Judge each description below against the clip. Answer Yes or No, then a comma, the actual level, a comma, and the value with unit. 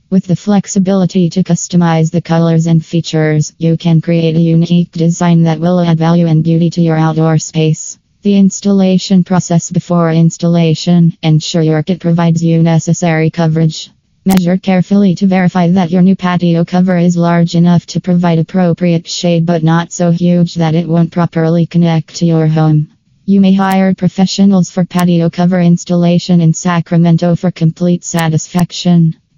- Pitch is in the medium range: Yes, medium, 170 Hz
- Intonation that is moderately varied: No, narrow, 1.5 semitones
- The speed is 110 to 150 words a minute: No, average, 160 wpm